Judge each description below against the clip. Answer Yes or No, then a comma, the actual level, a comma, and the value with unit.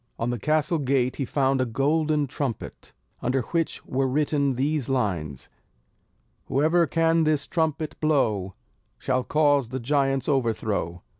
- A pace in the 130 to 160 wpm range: Yes, slow, 135 wpm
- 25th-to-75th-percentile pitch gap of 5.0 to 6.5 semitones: No, average, 3.6 semitones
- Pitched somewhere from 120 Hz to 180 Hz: Yes, low, 135 Hz